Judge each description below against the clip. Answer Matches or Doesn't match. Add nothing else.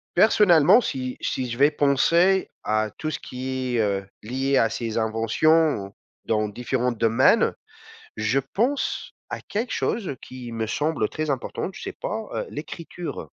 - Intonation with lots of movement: Matches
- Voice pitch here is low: Matches